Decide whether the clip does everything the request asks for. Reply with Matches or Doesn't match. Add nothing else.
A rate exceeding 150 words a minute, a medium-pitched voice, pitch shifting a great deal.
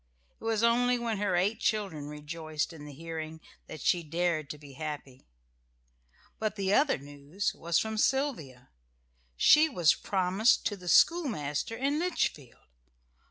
Doesn't match